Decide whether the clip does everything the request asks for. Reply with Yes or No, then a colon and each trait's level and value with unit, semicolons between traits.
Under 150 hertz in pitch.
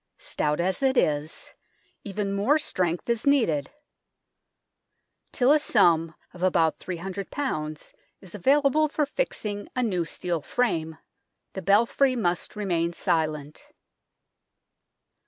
No: high, 190 Hz